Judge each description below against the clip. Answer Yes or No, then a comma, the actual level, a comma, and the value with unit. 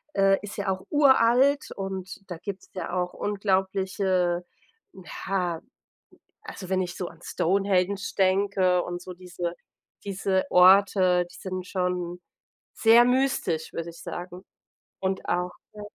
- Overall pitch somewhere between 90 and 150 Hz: No, high, 190 Hz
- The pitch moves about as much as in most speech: No, narrow, 1.8 semitones